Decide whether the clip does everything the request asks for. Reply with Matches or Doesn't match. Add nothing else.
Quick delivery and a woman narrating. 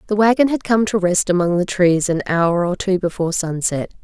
Matches